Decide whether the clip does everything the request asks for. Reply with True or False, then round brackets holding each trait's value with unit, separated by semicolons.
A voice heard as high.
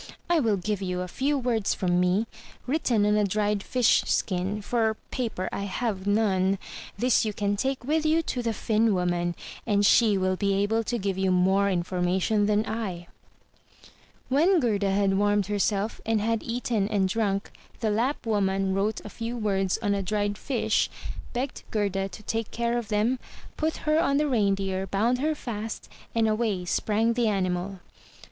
True (210 Hz)